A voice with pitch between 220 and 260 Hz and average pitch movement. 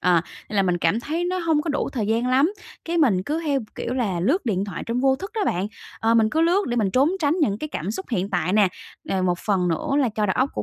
No: high, 230 Hz; wide, 7.6 semitones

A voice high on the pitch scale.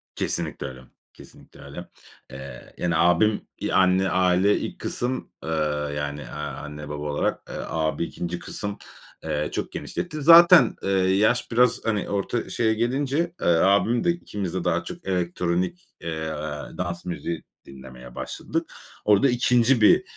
No: very low, 90 Hz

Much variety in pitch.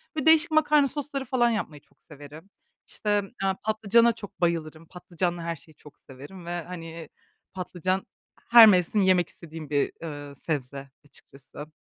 Yes: wide, 5.7 semitones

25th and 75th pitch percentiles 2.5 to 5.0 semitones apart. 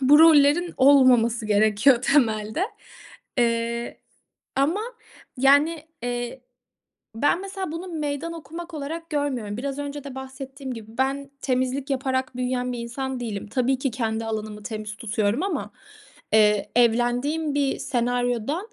Yes: average, 3.6 semitones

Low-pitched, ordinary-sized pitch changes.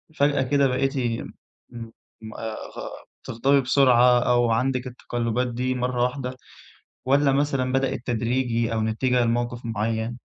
No: low, 125 Hz; narrow, 2.1 semitones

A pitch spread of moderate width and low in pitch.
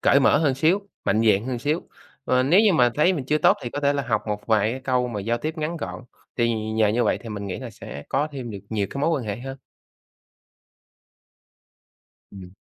Yes: average, 4.8 semitones; low, 125 Hz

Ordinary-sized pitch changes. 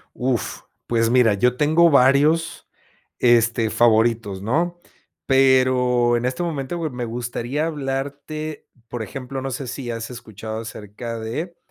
Yes: average, 3.1 semitones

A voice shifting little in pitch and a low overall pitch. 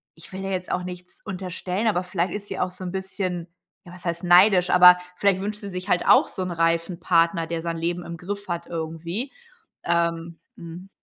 No: narrow, 1.9 semitones; medium, 180 Hz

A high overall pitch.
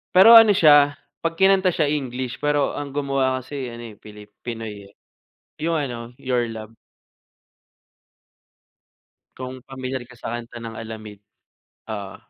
No: low, 130 Hz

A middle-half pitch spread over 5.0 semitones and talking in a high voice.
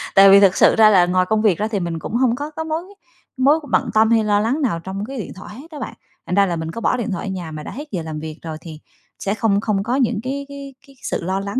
Yes: wide, 5.4 semitones; high, 205 Hz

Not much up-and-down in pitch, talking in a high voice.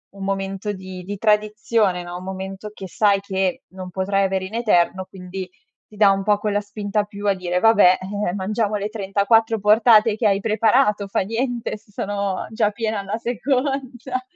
Yes: narrow, 2.3 semitones; high, 205 Hz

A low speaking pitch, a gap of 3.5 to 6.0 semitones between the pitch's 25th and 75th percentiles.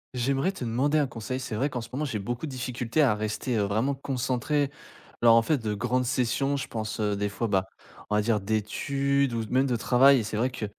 Yes: low, 125 Hz; average, 3.8 semitones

